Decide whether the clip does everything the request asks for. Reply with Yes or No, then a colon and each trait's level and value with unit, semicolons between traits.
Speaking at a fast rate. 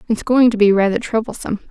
Yes: fast, 210 wpm